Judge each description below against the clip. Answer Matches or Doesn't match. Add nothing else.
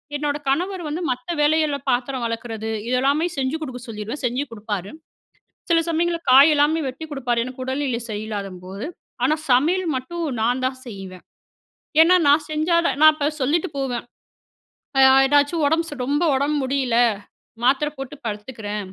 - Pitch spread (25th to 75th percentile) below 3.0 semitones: Doesn't match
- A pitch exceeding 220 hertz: Matches